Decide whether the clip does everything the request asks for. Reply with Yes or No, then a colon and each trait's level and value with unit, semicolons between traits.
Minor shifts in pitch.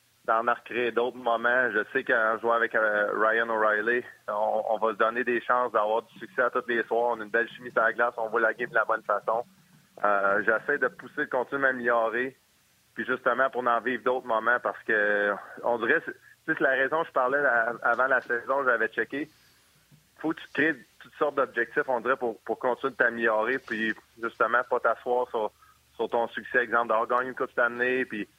Yes: narrow, 2.0 semitones